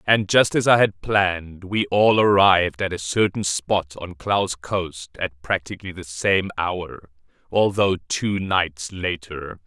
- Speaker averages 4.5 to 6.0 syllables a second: No, 3.8 syllables/s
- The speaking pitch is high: No, very low, 90 Hz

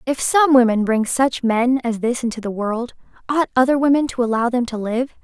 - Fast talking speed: Yes, fast, 220 wpm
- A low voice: No, high, 245 Hz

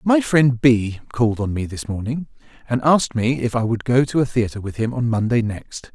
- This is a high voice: No, low, 120 Hz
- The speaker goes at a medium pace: No, fast, 230 wpm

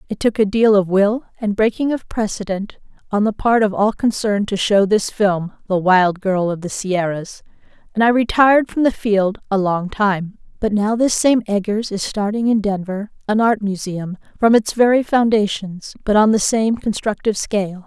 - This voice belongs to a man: No, female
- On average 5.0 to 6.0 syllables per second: No, 4.8 syllables/s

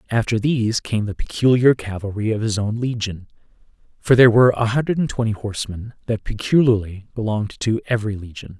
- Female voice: No, male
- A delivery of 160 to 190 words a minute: Yes, average, 170 wpm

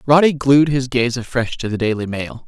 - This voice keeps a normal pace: No, fast, 220 wpm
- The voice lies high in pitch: No, low, 130 Hz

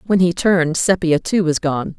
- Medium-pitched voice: Yes, medium, 170 Hz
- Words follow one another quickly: Yes, fast, 210 wpm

